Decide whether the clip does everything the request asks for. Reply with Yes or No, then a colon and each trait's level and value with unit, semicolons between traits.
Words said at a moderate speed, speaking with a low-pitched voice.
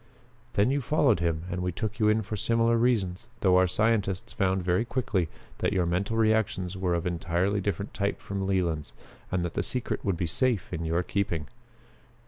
Yes: average, 190 wpm; very low, 95 Hz